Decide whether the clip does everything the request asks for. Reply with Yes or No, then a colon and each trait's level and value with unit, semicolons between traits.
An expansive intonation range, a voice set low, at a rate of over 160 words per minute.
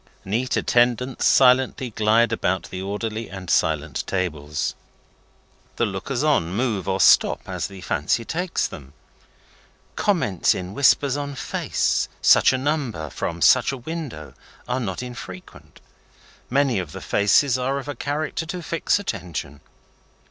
No: wide, 6.7 semitones; low, 115 Hz; average, 140 wpm